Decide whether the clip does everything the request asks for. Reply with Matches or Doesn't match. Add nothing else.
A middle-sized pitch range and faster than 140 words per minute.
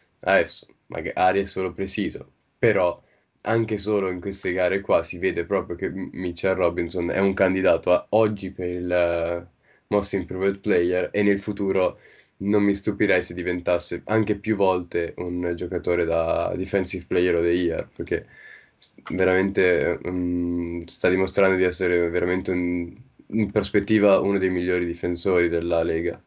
Doesn't match